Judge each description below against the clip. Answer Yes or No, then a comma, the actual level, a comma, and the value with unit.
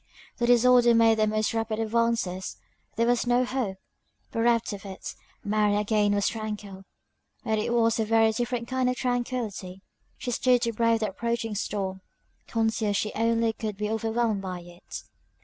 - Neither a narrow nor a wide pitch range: No, narrow, 2.2 semitones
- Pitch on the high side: Yes, high, 225 Hz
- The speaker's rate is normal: Yes, average, 165 wpm